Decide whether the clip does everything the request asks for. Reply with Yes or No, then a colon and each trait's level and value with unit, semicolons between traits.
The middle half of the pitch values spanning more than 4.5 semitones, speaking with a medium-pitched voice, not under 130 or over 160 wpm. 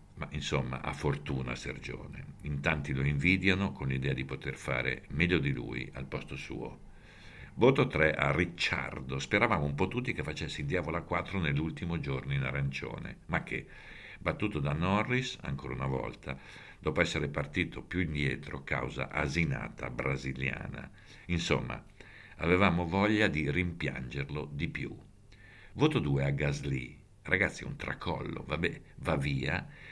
No: average, 5.3 semitones; very low, 75 Hz; average, 140 wpm